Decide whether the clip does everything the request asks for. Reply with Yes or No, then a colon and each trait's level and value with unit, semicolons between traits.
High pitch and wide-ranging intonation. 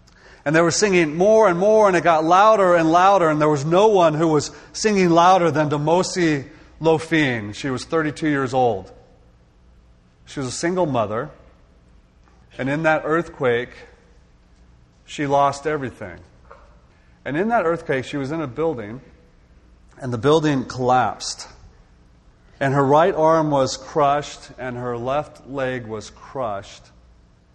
No: medium, 140 Hz; wide, 7.6 semitones